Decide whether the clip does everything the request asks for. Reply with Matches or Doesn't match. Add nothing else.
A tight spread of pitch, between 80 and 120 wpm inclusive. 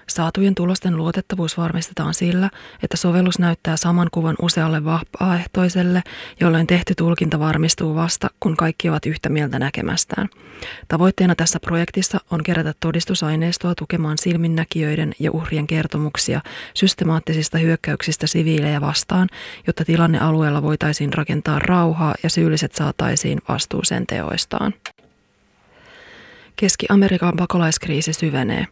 Matches